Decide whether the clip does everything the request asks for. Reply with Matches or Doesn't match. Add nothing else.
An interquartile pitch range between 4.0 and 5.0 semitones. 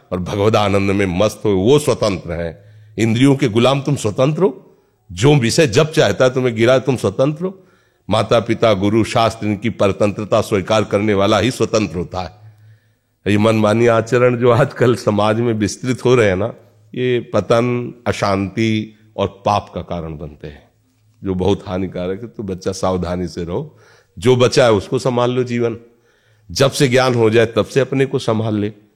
Doesn't match